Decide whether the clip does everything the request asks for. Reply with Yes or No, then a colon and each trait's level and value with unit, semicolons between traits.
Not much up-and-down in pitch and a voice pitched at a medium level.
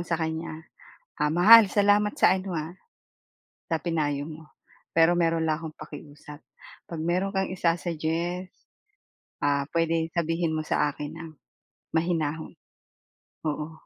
Yes: narrow, 2.0 semitones; medium, 165 Hz